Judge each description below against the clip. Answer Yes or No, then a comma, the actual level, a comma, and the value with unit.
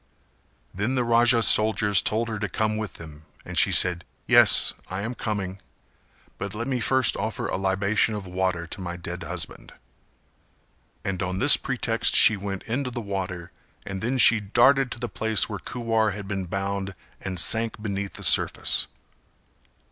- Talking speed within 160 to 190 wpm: Yes, average, 170 wpm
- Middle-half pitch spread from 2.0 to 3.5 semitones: Yes, average, 3.1 semitones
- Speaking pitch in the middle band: No, low, 105 Hz